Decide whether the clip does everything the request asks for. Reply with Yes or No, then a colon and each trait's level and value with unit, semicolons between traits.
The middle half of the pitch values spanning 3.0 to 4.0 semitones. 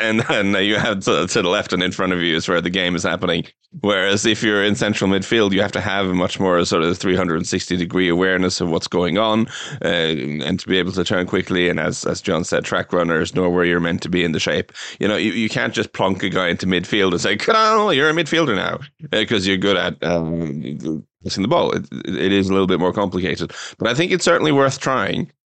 Yes: average, 3.6 semitones